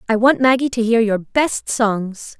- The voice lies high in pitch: Yes, high, 230 Hz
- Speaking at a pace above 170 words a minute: Yes, average, 200 wpm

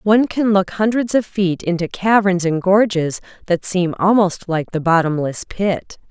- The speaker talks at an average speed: Yes, average, 165 wpm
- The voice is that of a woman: Yes, female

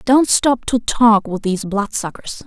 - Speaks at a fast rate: No, average, 170 wpm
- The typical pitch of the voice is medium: No, high, 220 Hz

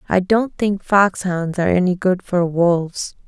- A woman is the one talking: Yes, female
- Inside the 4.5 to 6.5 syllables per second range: No, 4.3 syllables/s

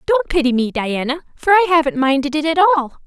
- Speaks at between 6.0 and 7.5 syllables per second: Yes, 6.4 syllables/s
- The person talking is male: No, female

